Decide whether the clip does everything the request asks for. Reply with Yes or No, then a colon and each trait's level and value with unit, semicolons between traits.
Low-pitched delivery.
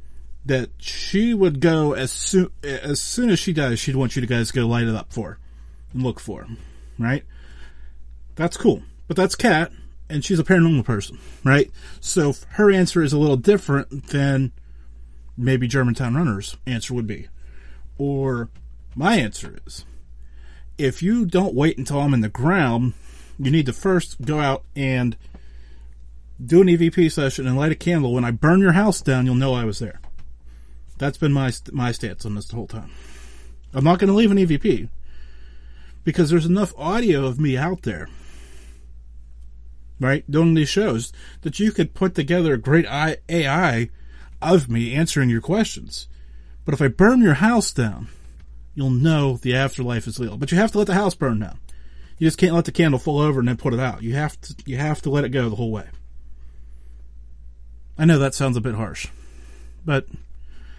Yes: low, 125 Hz